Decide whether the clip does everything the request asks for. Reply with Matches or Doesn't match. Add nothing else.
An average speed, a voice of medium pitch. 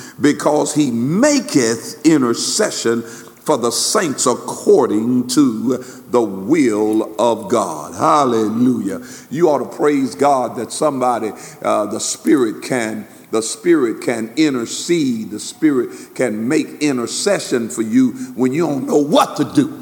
Doesn't match